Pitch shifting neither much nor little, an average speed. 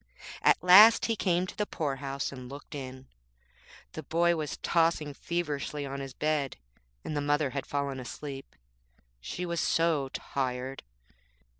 Yes: average, 3.7 semitones; average, 150 wpm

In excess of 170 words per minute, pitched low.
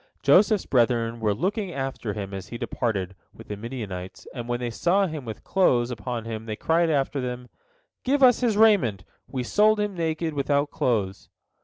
Yes: average, 180 wpm; low, 125 Hz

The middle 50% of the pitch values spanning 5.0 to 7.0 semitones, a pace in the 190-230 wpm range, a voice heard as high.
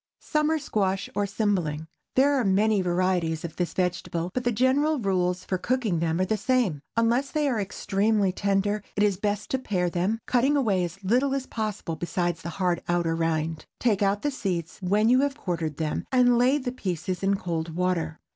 Yes: wide, 5.6 semitones; average, 195 wpm; high, 195 Hz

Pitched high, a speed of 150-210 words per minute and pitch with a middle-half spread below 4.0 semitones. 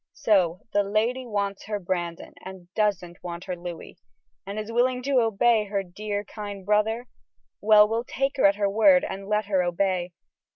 Yes: high, 205 Hz; average, 175 wpm; average, 2.9 semitones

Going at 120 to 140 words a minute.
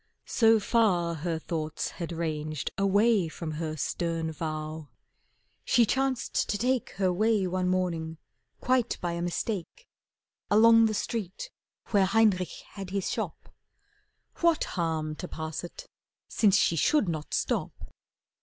Yes: slow, 135 wpm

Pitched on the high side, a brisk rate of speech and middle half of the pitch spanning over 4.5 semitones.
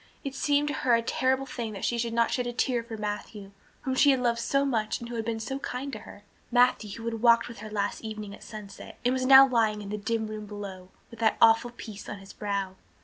No: high, 230 Hz; fast, 260 wpm; average, 2.9 semitones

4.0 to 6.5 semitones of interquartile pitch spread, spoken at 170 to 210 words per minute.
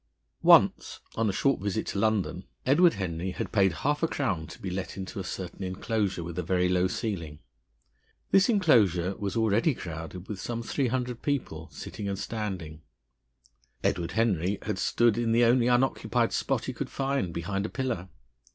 Yes: average, 4.7 semitones; average, 175 wpm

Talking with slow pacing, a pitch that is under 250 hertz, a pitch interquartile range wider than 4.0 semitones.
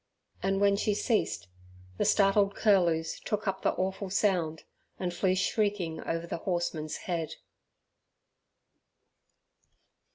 No: slow, 110 wpm; high, 190 Hz; average, 3.0 semitones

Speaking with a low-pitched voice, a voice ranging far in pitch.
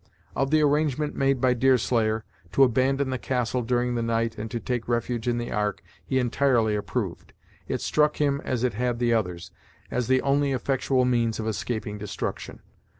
No: low, 125 Hz; average, 2.7 semitones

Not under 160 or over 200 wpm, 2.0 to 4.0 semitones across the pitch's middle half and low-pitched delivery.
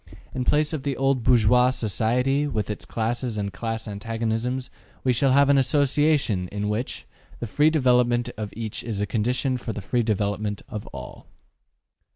Yes: average, 170 wpm; average, 3.7 semitones; low, 120 Hz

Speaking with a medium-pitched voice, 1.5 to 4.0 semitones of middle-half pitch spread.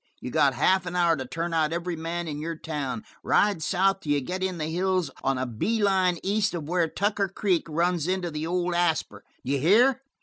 Yes: medium, 175 Hz; average, 3.3 semitones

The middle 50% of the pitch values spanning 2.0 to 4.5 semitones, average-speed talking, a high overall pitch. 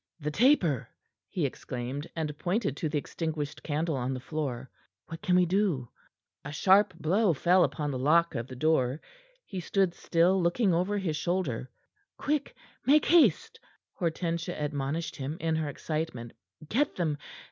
No: average, 4.0 semitones; average, 155 wpm; medium, 160 Hz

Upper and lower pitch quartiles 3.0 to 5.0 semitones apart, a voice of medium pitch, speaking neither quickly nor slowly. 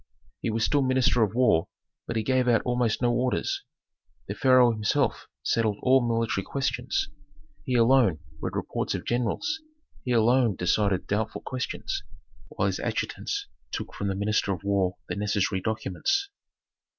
No: average, 3.8 semitones; low, 115 Hz; average, 150 wpm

